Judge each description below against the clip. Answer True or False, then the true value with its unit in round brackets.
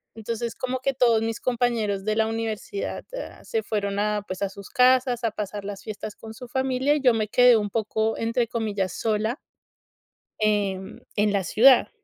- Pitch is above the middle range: True (225 Hz)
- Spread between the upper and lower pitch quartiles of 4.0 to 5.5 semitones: False (3.1 semitones)